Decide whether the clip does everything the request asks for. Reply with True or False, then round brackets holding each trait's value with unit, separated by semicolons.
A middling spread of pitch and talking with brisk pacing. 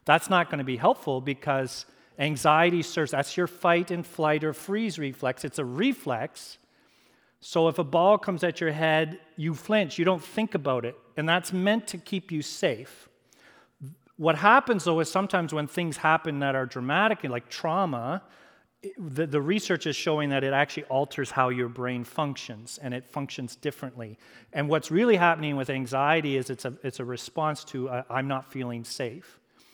False (4.5 semitones; 180 wpm)